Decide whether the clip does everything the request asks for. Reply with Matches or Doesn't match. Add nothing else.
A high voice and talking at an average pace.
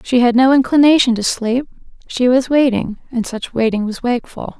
Matches